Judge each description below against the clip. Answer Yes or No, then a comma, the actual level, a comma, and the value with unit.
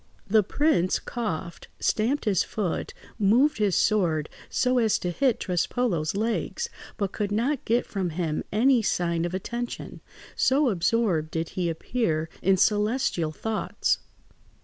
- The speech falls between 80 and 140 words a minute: Yes, slow, 135 wpm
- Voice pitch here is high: Yes, high, 205 Hz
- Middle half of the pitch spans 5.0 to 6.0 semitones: Yes, wide, 5.4 semitones